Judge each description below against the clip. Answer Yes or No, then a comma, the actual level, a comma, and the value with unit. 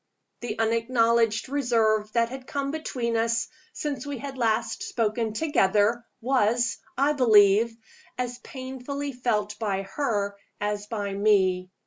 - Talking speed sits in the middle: No, slow, 125 wpm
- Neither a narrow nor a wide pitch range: Yes, average, 3.4 semitones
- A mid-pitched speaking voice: No, high, 230 Hz